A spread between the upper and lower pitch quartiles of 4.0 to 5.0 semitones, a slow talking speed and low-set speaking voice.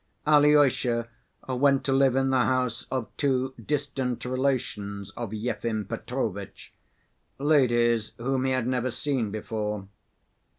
No: average, 2.7 semitones; slow, 120 wpm; low, 125 Hz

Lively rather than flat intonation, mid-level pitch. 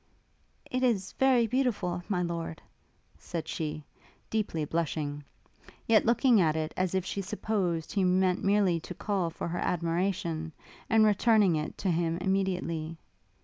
No: average, 3.9 semitones; medium, 180 Hz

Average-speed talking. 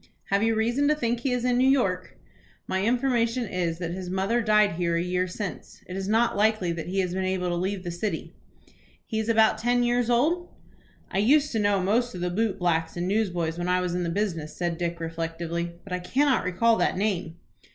No: fast, 225 wpm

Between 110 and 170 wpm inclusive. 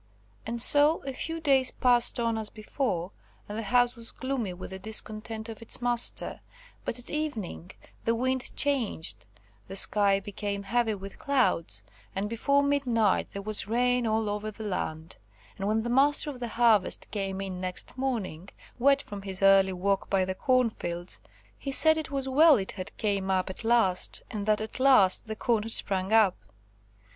No: average, 180 wpm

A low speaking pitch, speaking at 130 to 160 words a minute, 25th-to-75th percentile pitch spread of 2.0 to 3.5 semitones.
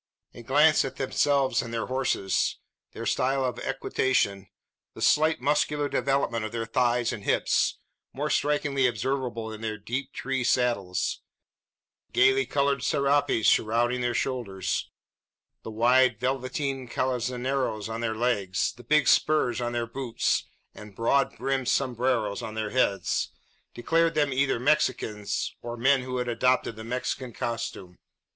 Yes: low, 125 Hz; average, 140 wpm; average, 2.9 semitones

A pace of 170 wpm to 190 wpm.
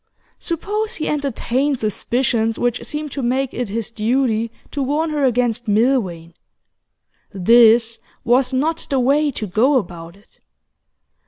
No: slow, 135 wpm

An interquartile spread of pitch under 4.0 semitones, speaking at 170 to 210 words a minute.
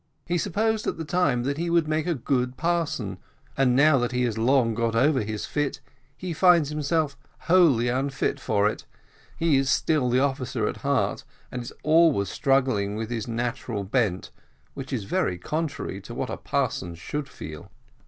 No: average, 5.1 semitones; average, 180 wpm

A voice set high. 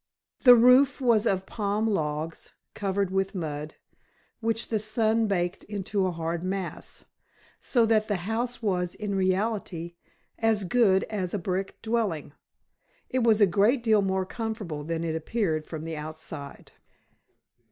Yes: high, 195 Hz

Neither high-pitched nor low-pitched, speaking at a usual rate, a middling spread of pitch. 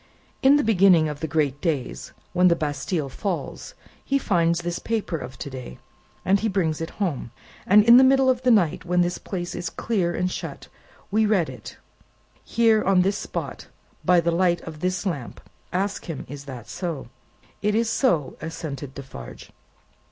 Yes: medium, 175 Hz; average, 180 wpm; average, 5.0 semitones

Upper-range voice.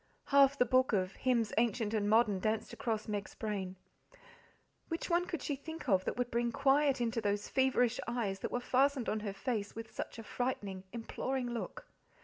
Yes: high, 235 Hz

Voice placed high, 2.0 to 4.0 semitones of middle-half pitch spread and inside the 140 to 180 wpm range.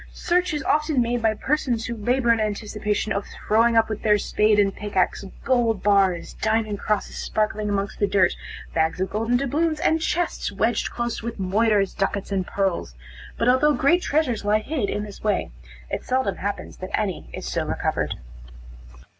Yes: high, 215 Hz; average, 3.5 semitones; average, 175 wpm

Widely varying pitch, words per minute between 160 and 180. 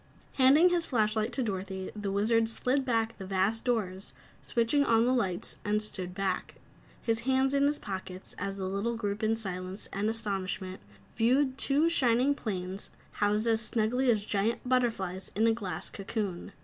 No: average, 3.8 semitones; average, 170 wpm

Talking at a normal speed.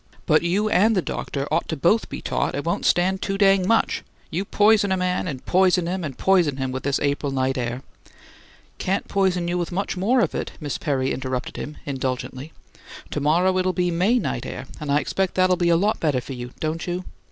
No: fast, 220 wpm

